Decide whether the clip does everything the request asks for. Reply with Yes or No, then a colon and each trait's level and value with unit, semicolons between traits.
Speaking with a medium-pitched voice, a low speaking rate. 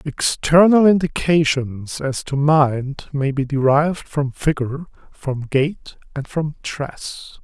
Yes: medium, 145 Hz; slow, 120 wpm